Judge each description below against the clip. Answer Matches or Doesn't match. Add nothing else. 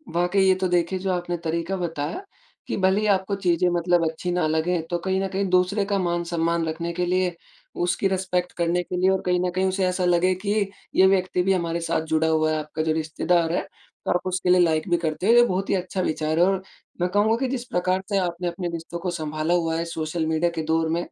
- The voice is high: Doesn't match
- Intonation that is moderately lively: Doesn't match